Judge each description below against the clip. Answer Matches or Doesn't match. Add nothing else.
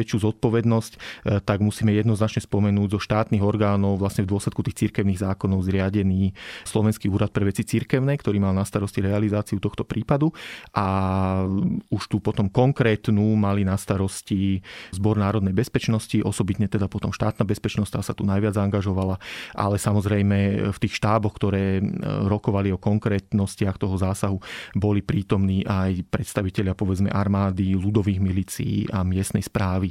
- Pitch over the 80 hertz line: Matches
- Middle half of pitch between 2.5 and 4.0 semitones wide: Doesn't match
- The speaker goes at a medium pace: Matches